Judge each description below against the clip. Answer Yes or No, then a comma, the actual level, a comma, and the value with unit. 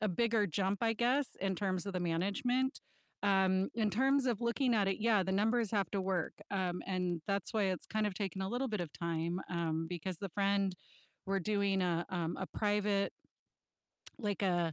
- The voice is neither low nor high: No, high, 195 Hz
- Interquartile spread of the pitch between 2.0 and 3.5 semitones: Yes, average, 2.8 semitones